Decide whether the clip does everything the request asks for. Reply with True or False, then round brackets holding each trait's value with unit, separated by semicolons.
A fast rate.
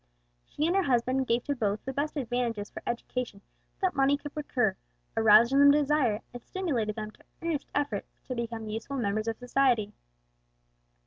False (180 wpm)